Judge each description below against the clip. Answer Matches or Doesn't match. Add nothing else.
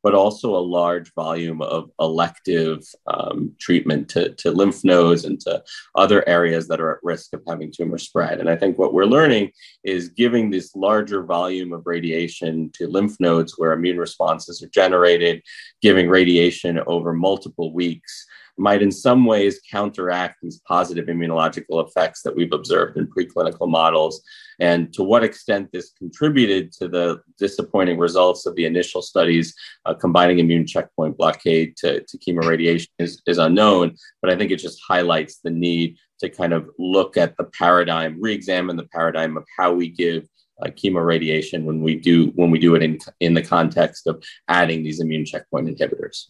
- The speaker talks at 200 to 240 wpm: Doesn't match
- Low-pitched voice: Matches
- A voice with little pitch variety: Matches